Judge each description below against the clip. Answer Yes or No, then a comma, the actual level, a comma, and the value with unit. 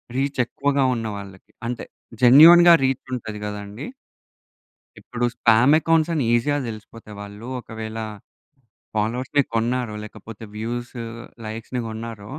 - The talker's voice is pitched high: No, low, 115 Hz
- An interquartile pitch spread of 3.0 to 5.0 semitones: Yes, average, 3.4 semitones